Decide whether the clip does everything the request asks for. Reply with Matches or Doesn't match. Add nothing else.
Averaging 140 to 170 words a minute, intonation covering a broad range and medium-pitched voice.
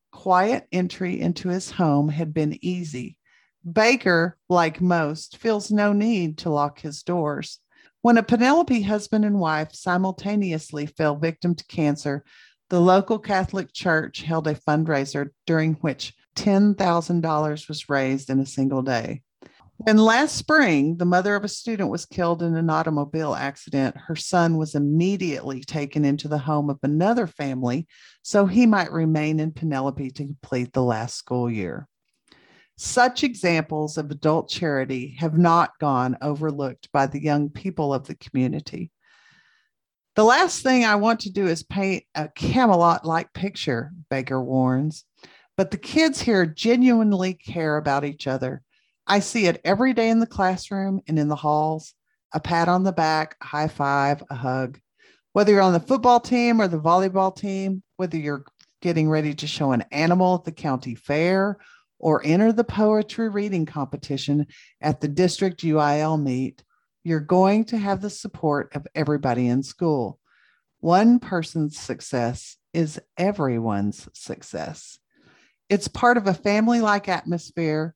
Doesn't match